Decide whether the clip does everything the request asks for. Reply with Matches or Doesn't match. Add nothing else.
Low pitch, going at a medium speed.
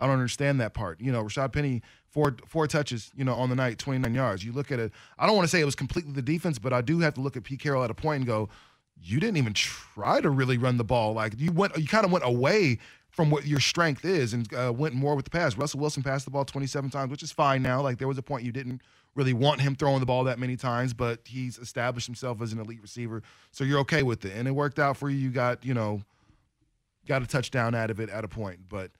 Doesn't match